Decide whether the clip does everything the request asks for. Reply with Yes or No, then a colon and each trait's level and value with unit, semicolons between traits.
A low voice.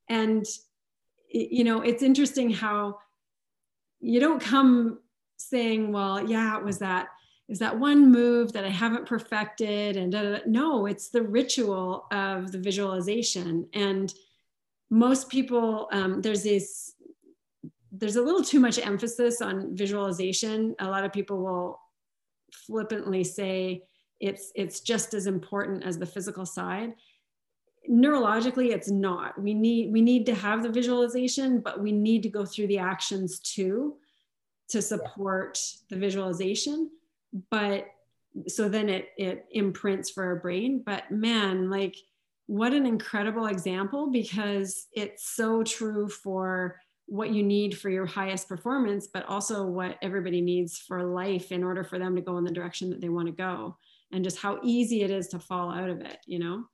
No: high, 205 Hz